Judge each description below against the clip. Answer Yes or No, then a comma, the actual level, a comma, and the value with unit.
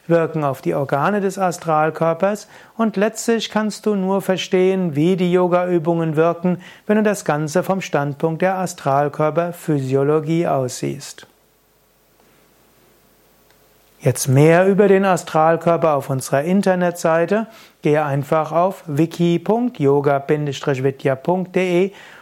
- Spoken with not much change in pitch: No, average, 3.7 semitones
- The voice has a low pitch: No, medium, 170 Hz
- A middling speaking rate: No, slow, 105 wpm